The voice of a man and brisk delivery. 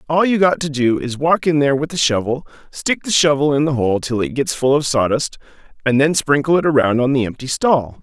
Yes: male; fast, 245 wpm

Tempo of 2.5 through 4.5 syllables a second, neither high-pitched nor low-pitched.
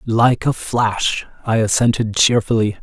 No: 4.1 syllables/s; low, 110 Hz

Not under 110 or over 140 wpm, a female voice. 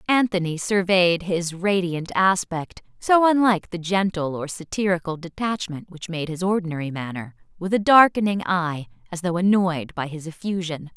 Yes: slow, 135 wpm; female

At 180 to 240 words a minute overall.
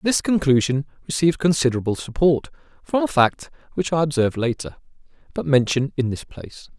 No: average, 150 wpm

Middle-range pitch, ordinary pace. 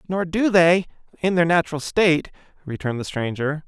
Yes: medium, 165 Hz; average, 165 wpm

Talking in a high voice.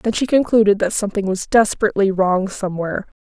Yes: high, 205 Hz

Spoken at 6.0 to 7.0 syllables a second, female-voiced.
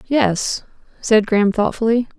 No: 4.3 syllables/s; female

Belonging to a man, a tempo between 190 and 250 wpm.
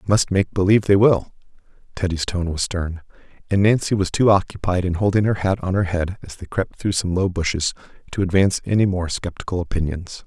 Yes: male; fast, 205 wpm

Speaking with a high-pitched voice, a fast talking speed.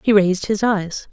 Yes: high, 200 Hz; fast, 215 wpm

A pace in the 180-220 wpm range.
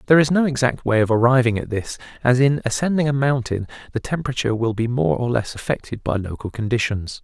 Yes: fast, 205 wpm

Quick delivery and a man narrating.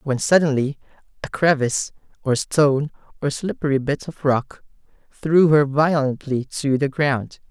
No: slow, 135 wpm; male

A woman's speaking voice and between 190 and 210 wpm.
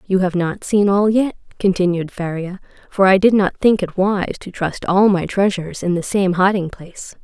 Yes: female; fast, 205 wpm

